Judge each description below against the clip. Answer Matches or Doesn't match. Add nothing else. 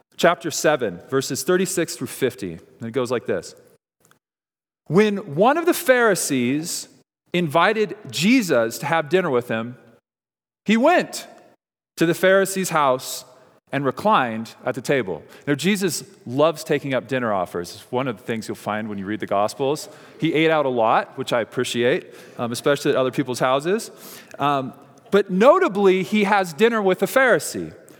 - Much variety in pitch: Matches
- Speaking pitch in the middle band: Matches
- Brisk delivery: Doesn't match